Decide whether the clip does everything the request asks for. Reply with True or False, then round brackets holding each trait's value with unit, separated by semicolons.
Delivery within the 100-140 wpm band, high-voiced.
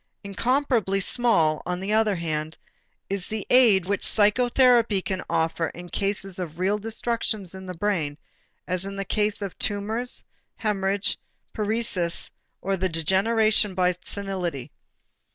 True (135 wpm; 195 Hz)